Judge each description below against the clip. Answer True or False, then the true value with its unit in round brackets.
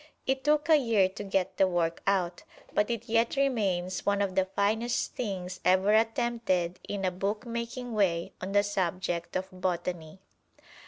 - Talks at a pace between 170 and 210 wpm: False (160 wpm)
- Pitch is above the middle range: True (200 Hz)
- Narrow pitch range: False (4.0 semitones)